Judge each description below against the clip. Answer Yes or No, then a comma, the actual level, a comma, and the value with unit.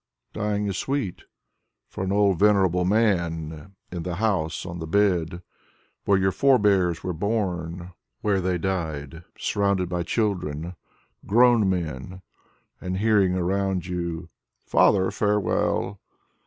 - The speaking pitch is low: Yes, very low, 95 Hz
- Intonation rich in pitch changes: No, average, 2.8 semitones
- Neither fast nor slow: No, slow, 125 wpm